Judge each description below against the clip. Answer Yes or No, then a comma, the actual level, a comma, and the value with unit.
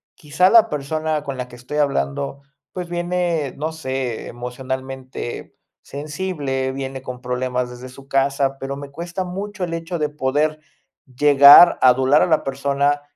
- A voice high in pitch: No, medium, 140 Hz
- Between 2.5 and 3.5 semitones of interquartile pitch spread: Yes, average, 3.2 semitones